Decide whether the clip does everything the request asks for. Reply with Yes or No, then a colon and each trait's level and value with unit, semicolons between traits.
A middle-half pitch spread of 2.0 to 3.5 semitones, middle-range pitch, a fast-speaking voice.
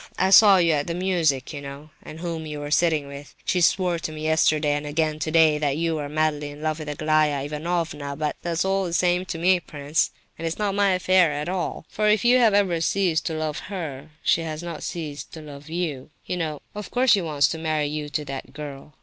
Yes: average, 3.0 semitones; medium, 155 Hz; fast, 235 wpm